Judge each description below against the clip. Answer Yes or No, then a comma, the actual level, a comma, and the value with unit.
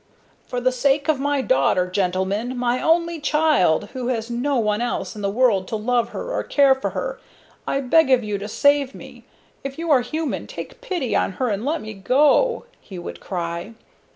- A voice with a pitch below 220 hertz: No, very high, 250 Hz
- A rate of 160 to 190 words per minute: No, average, 200 wpm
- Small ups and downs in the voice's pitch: No, wide, 5.5 semitones